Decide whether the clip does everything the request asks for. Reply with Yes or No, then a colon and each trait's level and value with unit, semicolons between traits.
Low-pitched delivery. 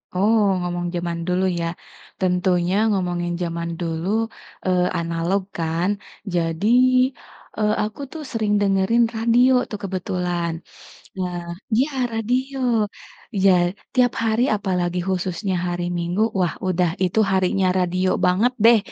No: medium, 185 Hz